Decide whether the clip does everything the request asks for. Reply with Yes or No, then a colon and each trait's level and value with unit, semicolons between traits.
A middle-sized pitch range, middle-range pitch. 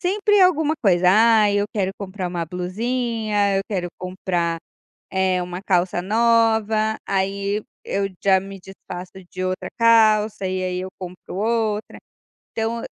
No: average, 3.2 semitones; high, 200 Hz